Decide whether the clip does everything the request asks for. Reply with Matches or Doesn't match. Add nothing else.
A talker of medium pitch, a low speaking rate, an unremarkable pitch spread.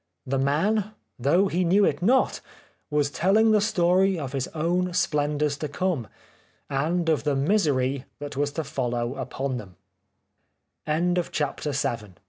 Matches